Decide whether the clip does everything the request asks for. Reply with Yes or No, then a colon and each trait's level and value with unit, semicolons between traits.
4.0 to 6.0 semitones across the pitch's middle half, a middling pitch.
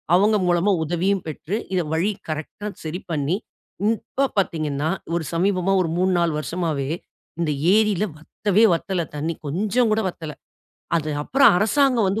Yes: average, 4.5 semitones; medium, 180 Hz